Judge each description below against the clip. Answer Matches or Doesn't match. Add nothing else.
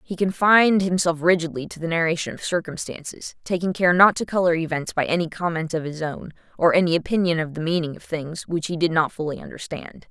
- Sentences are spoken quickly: Matches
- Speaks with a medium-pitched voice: Matches